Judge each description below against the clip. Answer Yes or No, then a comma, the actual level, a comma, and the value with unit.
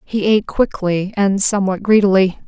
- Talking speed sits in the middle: Yes, average, 145 wpm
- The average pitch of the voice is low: No, high, 195 Hz